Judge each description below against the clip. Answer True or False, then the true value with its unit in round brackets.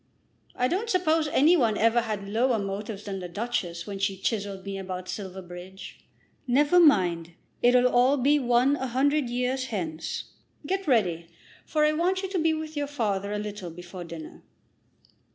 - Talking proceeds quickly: False (170 wpm)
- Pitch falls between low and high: False (230 Hz)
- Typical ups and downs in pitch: False (7.0 semitones)